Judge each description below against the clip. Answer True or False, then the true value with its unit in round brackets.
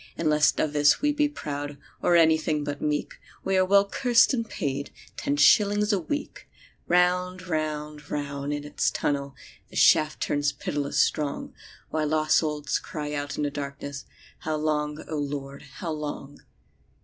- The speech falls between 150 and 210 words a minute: True (160 wpm)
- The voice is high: False (150 Hz)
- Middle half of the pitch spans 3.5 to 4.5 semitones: False (3.1 semitones)